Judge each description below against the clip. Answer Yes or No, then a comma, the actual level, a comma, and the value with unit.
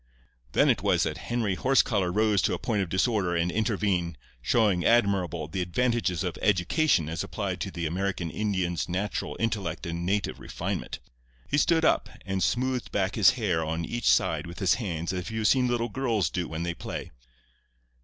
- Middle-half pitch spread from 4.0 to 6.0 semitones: Yes, average, 4.7 semitones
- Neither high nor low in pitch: No, very low, 95 Hz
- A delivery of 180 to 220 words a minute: Yes, average, 185 wpm